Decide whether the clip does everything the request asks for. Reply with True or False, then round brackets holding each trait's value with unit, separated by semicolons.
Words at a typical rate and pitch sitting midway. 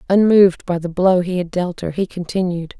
False (215 wpm; 180 Hz)